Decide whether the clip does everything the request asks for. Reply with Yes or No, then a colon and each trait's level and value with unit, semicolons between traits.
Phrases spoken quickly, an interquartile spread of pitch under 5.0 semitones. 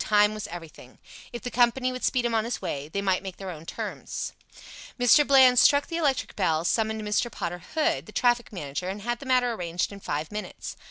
No: fast, 215 wpm; wide, 5.6 semitones